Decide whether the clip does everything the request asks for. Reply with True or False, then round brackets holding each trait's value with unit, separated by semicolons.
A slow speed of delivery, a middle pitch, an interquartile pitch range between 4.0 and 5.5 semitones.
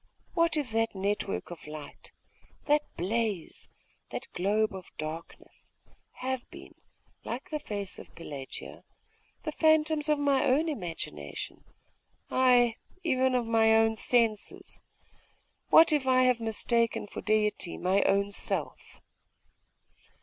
False (120 wpm; 225 Hz; 4.8 semitones)